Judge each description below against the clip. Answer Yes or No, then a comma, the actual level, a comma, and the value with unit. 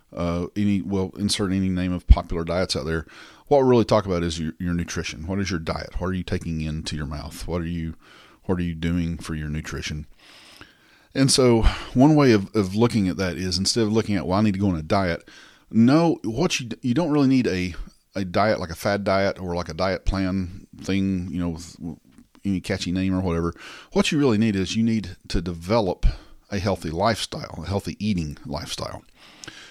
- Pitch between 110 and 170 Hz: No, very low, 95 Hz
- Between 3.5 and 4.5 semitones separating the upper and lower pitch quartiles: Yes, average, 3.8 semitones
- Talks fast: Yes, fast, 215 wpm